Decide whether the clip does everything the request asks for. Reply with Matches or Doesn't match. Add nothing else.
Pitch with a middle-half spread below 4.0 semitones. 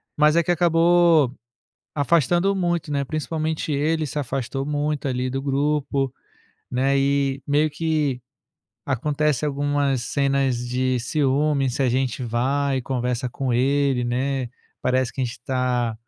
Matches